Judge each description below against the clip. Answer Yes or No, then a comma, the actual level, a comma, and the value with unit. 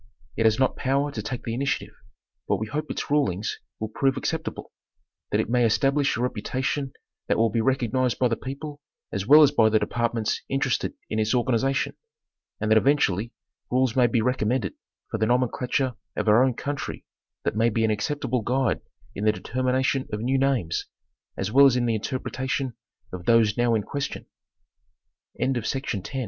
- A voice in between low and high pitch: No, low, 125 Hz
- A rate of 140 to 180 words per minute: Yes, average, 170 wpm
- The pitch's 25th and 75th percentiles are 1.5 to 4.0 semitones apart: Yes, average, 3.3 semitones